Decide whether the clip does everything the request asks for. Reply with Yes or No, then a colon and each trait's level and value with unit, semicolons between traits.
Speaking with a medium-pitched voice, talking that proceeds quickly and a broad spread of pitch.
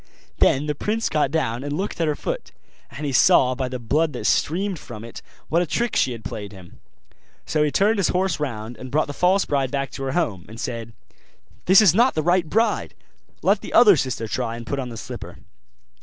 Yes: medium, 145 Hz; fast, 225 wpm; wide, 6.4 semitones